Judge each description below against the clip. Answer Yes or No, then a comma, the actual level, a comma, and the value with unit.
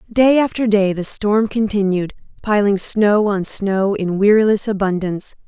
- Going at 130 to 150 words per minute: Yes, average, 140 wpm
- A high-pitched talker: Yes, high, 205 Hz